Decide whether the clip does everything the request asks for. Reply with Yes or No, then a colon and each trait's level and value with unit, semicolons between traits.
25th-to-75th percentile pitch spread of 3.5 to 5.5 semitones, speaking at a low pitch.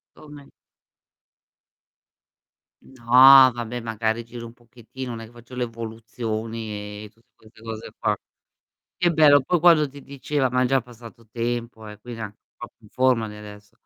No: narrow, 2.5 semitones; low, 115 Hz